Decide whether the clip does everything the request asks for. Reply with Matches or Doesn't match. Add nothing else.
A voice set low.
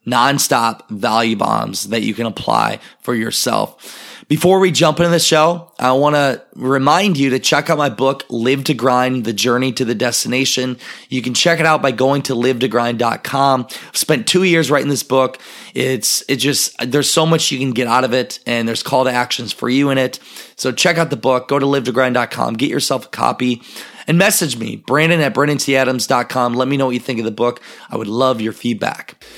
Matches